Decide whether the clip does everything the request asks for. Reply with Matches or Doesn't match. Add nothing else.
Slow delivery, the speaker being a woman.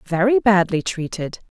Matches